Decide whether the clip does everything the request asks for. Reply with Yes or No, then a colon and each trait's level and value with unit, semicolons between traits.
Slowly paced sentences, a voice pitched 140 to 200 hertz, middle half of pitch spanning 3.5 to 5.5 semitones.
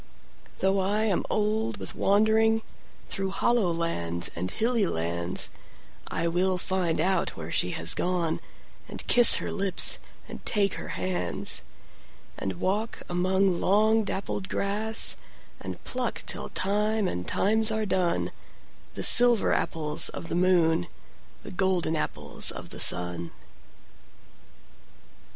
Yes: slow, 110 wpm; high, 190 Hz; average, 4.5 semitones